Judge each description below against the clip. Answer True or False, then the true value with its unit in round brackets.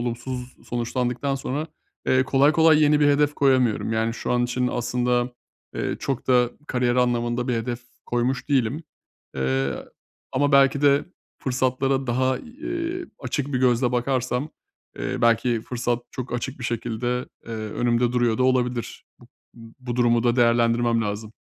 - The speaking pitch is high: False (125 Hz)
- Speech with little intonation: True (1.9 semitones)